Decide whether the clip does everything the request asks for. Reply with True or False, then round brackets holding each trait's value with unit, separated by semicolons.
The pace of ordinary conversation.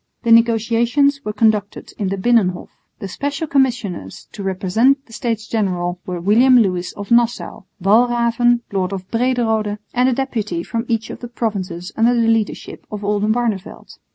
True (155 wpm)